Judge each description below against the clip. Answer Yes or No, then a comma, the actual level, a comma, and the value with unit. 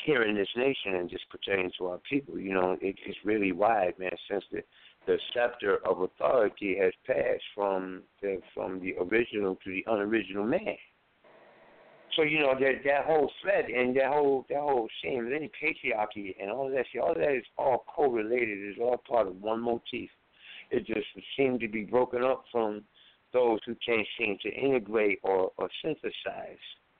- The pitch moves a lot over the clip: Yes, wide, 5.7 semitones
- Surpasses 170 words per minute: Yes, average, 185 wpm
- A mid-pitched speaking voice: No, low, 110 Hz